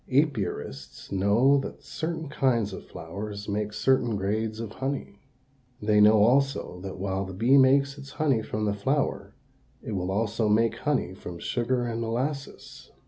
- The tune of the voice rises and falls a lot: No, average, 4.9 semitones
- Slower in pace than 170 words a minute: Yes, average, 155 wpm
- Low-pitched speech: Yes, low, 115 Hz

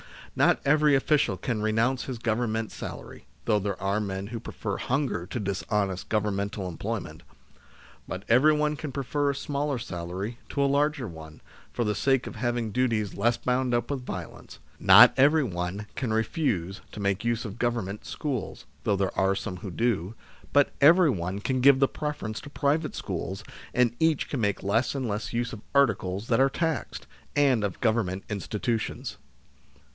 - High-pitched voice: No, low, 115 Hz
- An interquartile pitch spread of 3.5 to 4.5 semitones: No, average, 5.3 semitones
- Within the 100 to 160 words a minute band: No, average, 170 wpm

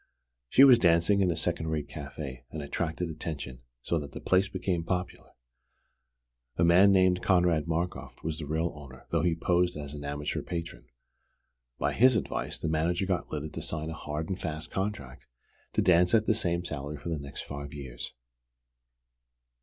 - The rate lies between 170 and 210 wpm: Yes, average, 175 wpm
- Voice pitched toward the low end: Yes, very low, 80 Hz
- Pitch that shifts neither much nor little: Yes, average, 3.4 semitones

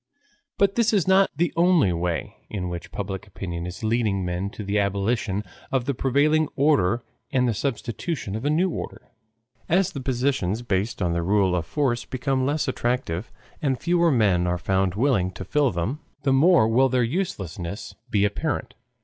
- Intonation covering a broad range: Yes, wide, 6.7 semitones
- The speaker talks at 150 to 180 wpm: Yes, average, 175 wpm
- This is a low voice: Yes, low, 115 Hz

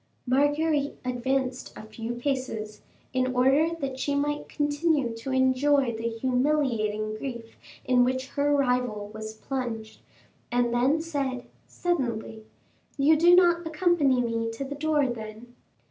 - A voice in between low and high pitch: No, very high, 260 Hz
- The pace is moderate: No, slow, 130 wpm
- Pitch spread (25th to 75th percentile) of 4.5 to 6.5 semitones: No, average, 3.7 semitones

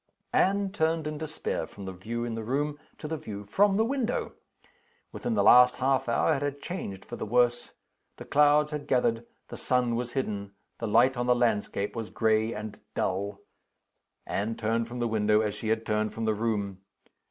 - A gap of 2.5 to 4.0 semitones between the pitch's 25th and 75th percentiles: No, average, 5.2 semitones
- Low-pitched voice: Yes, low, 120 Hz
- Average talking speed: Yes, average, 195 wpm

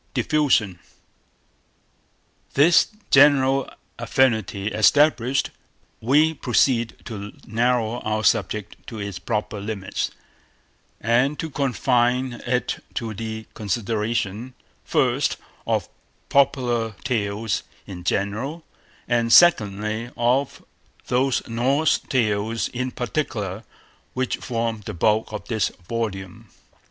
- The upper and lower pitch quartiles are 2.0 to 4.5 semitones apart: Yes, average, 3.4 semitones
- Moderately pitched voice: No, low, 115 Hz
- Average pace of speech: No, slow, 95 wpm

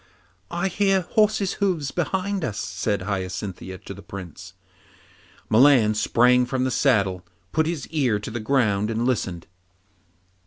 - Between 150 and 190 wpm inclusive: No, average, 140 wpm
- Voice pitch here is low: Yes, low, 120 Hz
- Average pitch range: No, wide, 8.0 semitones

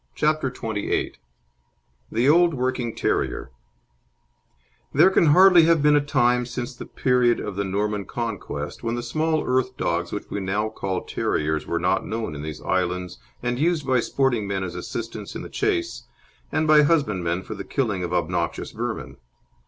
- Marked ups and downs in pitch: Yes, wide, 7.2 semitones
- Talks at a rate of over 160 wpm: Yes, average, 170 wpm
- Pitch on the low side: Yes, low, 120 Hz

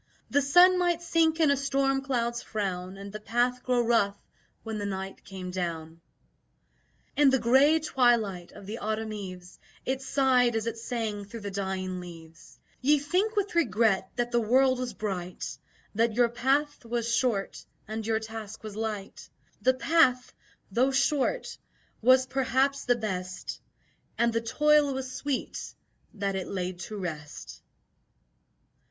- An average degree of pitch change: Yes, average, 5.0 semitones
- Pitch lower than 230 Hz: No, high, 235 Hz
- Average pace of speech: Yes, average, 150 wpm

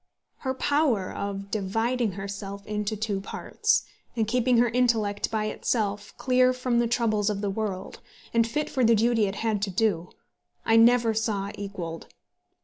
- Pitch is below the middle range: No, high, 220 Hz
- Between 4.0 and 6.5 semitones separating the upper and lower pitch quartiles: No, average, 3.0 semitones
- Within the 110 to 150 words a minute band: No, average, 160 wpm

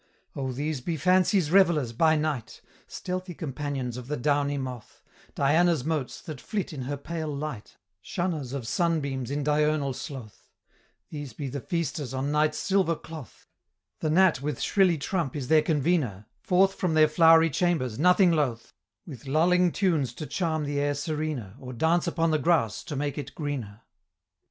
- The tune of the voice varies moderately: Yes, average, 3.7 semitones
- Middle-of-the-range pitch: Yes, medium, 150 Hz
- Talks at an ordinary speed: Yes, average, 165 wpm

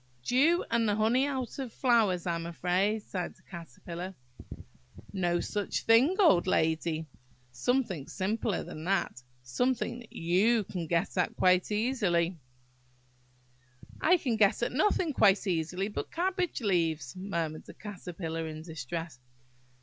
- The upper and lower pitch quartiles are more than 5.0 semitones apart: Yes, wide, 5.6 semitones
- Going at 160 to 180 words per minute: No, slow, 135 wpm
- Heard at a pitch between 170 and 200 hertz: Yes, high, 190 Hz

